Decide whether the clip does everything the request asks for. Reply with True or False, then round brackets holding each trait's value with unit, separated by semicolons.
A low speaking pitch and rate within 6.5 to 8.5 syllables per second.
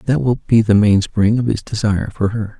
False (110 Hz; 5.5 syllables/s)